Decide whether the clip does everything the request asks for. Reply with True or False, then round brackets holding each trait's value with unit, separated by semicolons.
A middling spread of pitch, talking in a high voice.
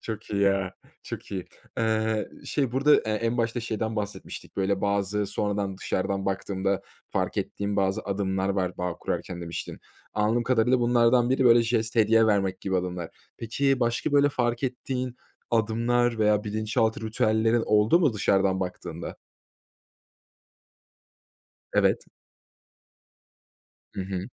False (3.2 semitones; 110 Hz)